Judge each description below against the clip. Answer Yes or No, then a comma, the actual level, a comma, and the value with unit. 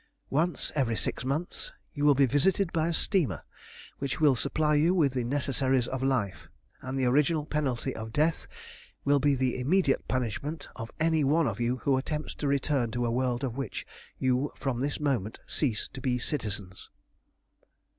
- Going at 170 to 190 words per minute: Yes, average, 175 wpm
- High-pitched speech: No, low, 135 Hz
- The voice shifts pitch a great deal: No, average, 3.3 semitones